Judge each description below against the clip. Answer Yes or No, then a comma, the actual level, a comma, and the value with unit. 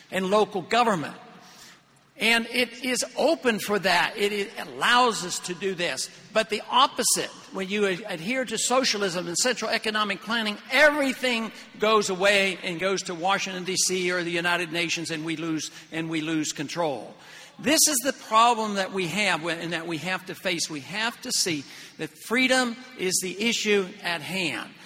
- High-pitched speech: Yes, high, 195 Hz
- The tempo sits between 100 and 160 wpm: No, average, 170 wpm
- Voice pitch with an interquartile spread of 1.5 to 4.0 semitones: No, average, 4.8 semitones